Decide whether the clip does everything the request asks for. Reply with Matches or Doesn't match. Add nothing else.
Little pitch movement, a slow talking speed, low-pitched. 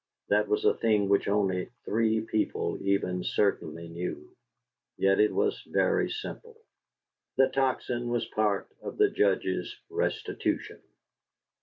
Doesn't match